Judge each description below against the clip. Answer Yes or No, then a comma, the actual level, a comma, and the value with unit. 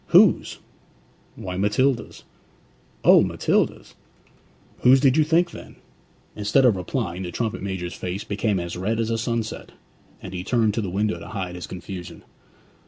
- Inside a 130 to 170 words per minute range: Yes, average, 150 wpm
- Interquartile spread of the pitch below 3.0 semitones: No, average, 4.3 semitones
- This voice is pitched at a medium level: No, low, 105 Hz